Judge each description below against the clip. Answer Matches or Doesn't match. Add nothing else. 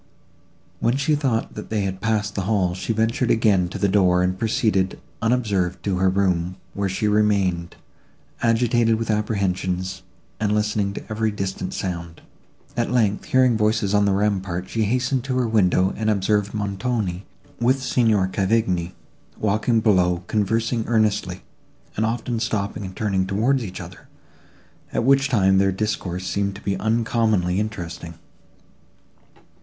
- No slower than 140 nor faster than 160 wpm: Matches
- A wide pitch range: Doesn't match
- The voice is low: Matches